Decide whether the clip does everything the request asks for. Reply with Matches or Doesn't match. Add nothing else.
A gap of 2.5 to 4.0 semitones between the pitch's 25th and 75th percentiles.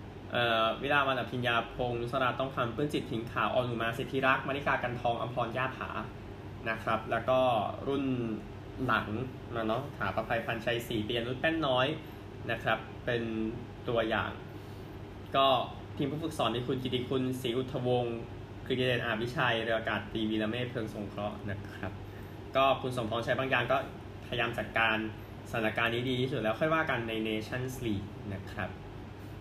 Matches